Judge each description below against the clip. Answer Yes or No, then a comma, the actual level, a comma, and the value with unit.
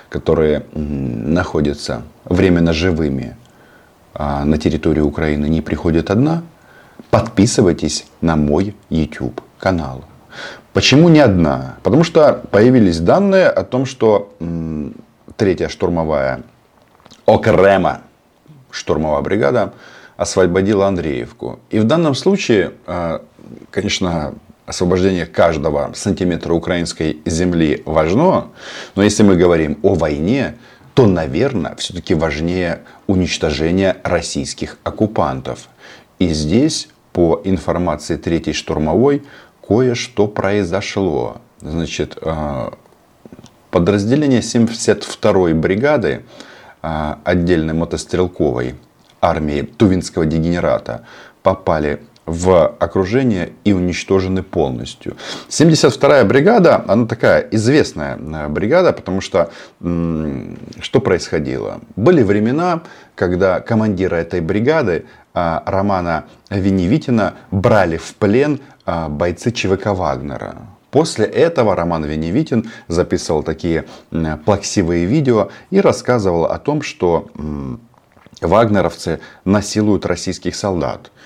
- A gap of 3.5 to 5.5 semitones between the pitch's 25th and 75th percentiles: Yes, average, 4.1 semitones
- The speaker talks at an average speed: No, slow, 90 wpm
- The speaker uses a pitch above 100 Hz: No, very low, 90 Hz